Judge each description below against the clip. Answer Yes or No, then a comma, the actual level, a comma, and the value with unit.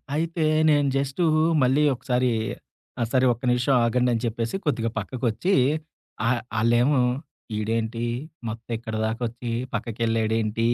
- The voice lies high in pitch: No, low, 120 Hz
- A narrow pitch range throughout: Yes, narrow, 2.2 semitones